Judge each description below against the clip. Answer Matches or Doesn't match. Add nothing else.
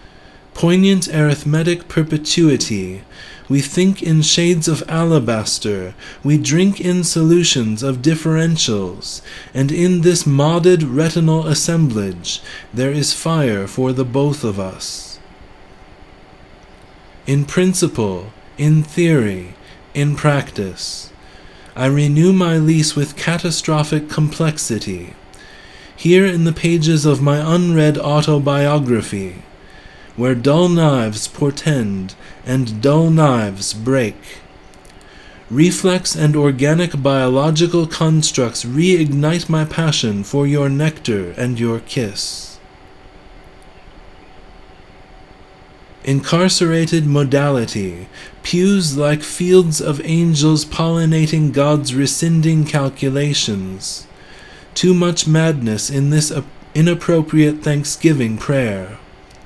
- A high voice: Doesn't match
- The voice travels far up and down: Matches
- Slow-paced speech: Matches